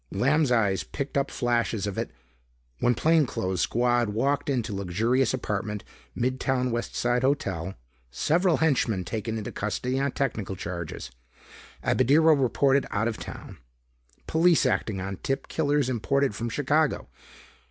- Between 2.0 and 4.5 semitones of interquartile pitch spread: No, average, 5.2 semitones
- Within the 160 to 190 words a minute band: No, average, 140 wpm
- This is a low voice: Yes, low, 120 Hz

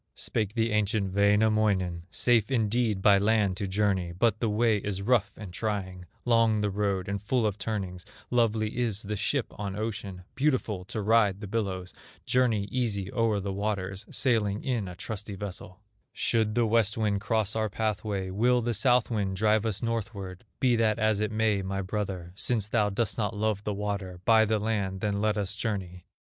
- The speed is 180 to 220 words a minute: Yes, average, 185 wpm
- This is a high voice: No, low, 105 Hz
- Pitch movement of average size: No, narrow, 2.3 semitones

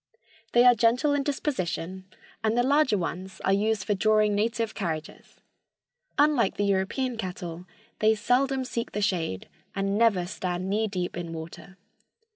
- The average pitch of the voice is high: Yes, high, 205 Hz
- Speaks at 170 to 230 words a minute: No, average, 150 wpm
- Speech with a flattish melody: No, average, 4.3 semitones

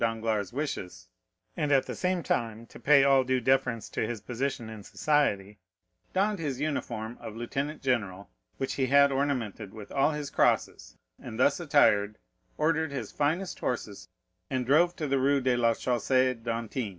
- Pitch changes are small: No, average, 4.1 semitones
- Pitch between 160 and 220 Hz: No, low, 130 Hz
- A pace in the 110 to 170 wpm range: Yes, average, 160 wpm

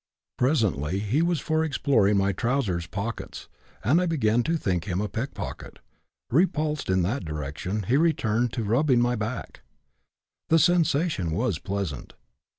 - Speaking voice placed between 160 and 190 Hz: No, low, 115 Hz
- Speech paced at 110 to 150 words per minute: Yes, average, 145 wpm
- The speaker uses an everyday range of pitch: No, wide, 7.4 semitones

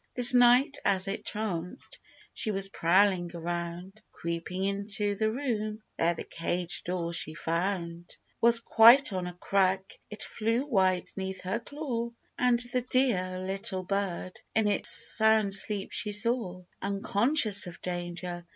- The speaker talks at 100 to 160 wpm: Yes, average, 140 wpm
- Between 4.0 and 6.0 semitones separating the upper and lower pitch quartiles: No, average, 3.6 semitones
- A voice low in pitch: No, high, 195 Hz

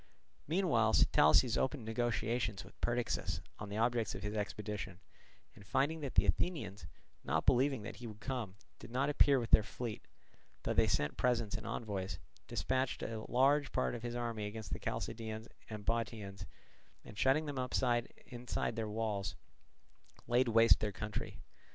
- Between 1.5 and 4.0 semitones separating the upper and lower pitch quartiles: Yes, average, 3.0 semitones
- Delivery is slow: No, average, 160 wpm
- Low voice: Yes, low, 115 Hz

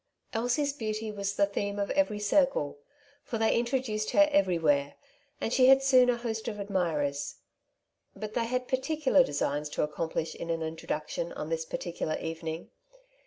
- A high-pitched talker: Yes, high, 210 Hz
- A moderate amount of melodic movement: No, wide, 7.3 semitones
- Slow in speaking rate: No, average, 160 wpm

